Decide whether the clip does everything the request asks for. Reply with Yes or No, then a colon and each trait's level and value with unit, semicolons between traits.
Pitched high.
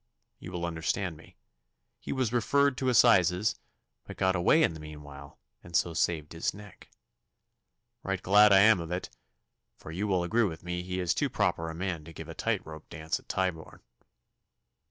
No: very low, 90 Hz